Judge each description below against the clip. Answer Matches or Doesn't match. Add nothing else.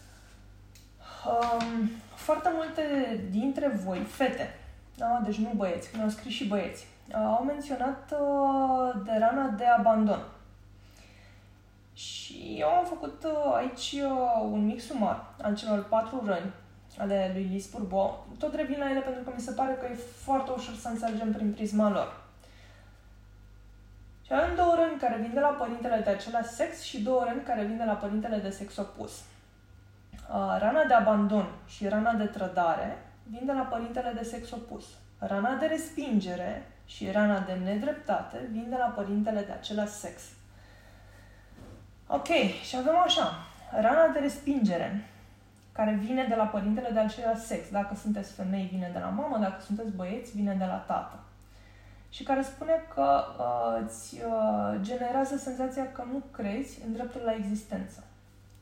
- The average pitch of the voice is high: Matches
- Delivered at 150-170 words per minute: Matches